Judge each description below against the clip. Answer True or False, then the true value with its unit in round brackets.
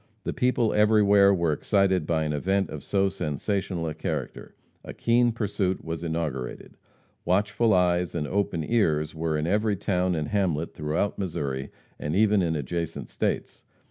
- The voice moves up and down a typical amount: True (4.4 semitones)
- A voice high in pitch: False (90 Hz)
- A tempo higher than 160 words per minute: False (155 wpm)